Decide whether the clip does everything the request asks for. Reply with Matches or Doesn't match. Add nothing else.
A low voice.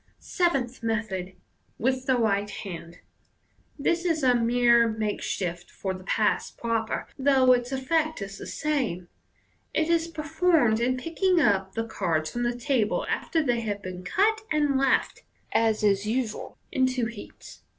Doesn't match